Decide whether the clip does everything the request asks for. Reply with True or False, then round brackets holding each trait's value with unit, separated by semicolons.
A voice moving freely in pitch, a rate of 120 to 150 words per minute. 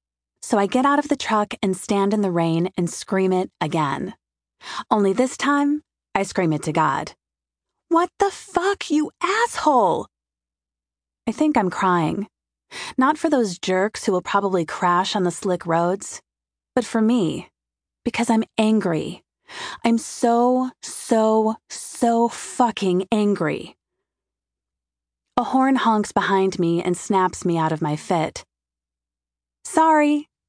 True (6.9 semitones; 140 wpm)